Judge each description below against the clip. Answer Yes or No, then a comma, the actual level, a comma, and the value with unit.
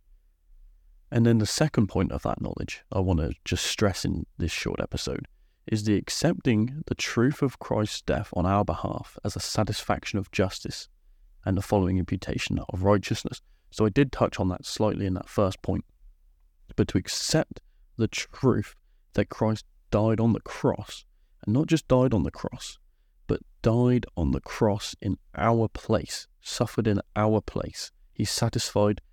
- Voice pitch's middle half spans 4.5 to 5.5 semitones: Yes, average, 4.9 semitones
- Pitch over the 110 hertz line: No, low, 100 Hz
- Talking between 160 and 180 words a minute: Yes, average, 170 wpm